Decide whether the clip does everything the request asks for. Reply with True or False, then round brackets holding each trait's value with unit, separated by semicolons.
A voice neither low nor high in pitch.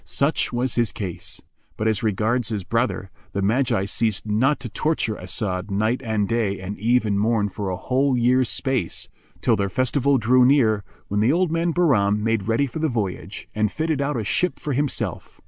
False (115 Hz)